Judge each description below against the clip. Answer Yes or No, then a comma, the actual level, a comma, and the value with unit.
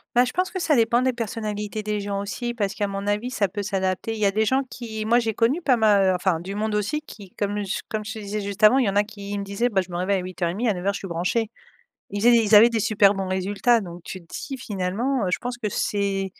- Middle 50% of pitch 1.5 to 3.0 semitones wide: Yes, average, 2.7 semitones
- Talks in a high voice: Yes, high, 210 Hz